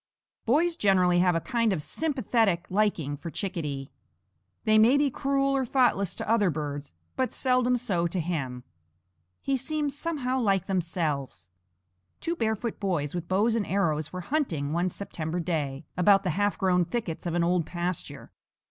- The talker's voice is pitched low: No, medium, 185 Hz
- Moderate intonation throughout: No, wide, 6.4 semitones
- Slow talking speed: No, average, 160 wpm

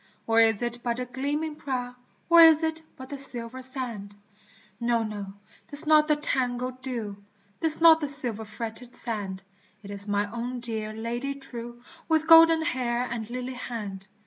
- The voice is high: Yes, high, 245 Hz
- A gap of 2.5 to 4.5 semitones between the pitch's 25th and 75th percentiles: Yes, average, 3.7 semitones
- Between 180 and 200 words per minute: No, average, 170 wpm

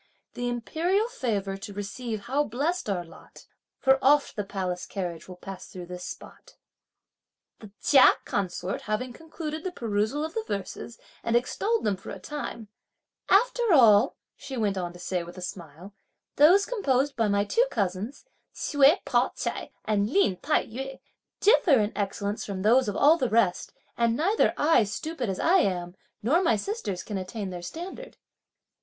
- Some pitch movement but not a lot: No, wide, 7.4 semitones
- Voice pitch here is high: Yes, high, 230 Hz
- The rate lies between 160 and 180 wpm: Yes, average, 170 wpm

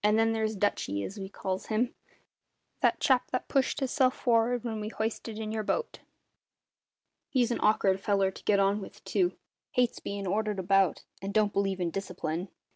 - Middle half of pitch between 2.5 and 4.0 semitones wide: Yes, average, 2.8 semitones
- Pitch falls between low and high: No, high, 210 Hz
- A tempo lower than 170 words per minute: No, average, 175 wpm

